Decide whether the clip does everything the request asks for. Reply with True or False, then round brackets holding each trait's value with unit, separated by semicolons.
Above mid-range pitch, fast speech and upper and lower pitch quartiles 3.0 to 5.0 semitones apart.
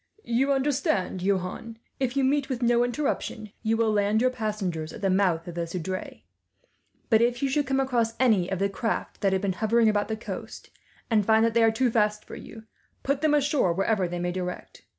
True (220 Hz; 210 wpm; 4.6 semitones)